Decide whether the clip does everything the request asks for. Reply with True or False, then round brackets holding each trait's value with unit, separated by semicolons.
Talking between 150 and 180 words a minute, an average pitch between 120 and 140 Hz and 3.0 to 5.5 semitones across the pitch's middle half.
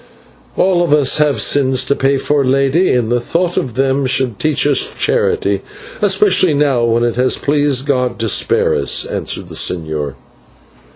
True (175 wpm; 135 Hz; 3.5 semitones)